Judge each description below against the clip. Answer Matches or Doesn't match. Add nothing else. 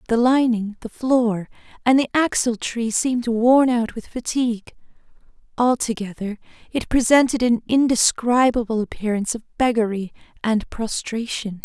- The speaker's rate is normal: Doesn't match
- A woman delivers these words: Matches